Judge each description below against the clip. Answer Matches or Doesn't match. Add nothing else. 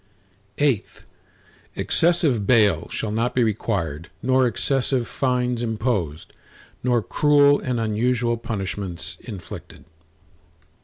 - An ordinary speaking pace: Doesn't match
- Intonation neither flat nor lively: Matches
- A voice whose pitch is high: Doesn't match